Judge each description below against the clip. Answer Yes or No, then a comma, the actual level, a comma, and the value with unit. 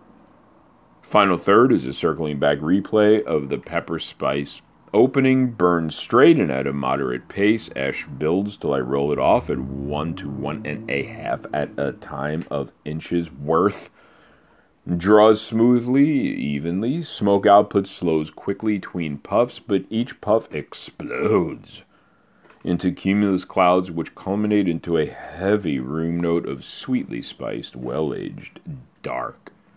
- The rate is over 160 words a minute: No, slow, 135 wpm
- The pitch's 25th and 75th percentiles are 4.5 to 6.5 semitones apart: Yes, wide, 5.5 semitones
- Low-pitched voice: Yes, very low, 90 Hz